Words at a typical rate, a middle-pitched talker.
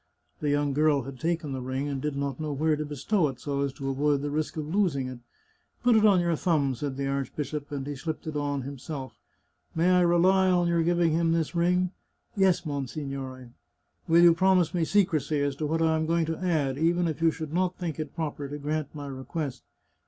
No: fast, 235 wpm; medium, 155 Hz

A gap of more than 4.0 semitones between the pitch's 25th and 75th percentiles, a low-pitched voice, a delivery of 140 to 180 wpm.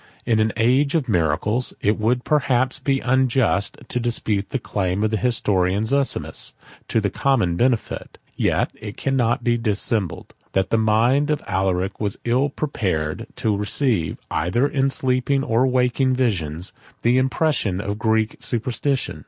Yes: average, 4.4 semitones; low, 115 Hz; average, 150 wpm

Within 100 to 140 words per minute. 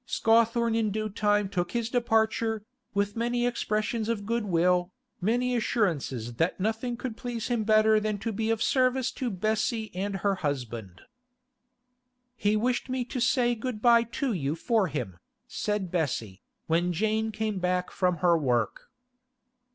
No: average, 150 wpm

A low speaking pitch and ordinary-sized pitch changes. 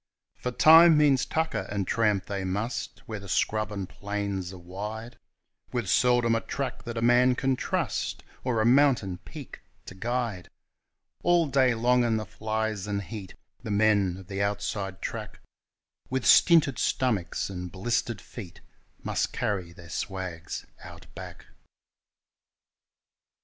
Yes: low, 110 Hz; average, 4.3 semitones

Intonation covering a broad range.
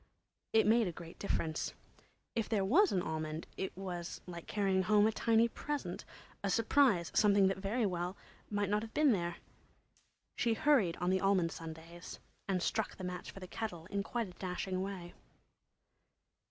No: average, 3.8 semitones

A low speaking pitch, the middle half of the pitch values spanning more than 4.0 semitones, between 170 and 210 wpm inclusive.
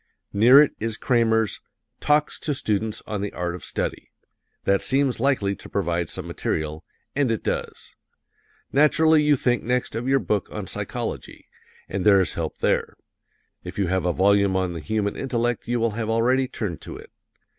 Yes: low, 110 Hz; average, 4.6 semitones; average, 175 wpm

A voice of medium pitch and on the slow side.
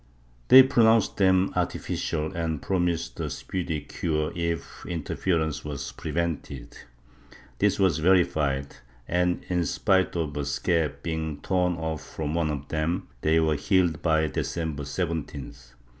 No: very low, 80 Hz; slow, 130 wpm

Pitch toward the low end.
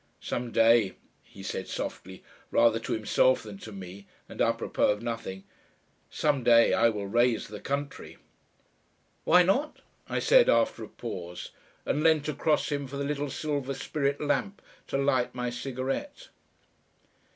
Yes: low, 125 Hz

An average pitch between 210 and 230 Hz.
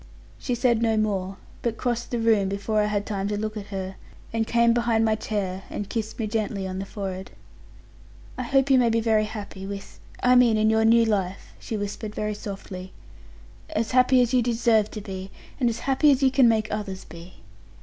Yes: high, 215 Hz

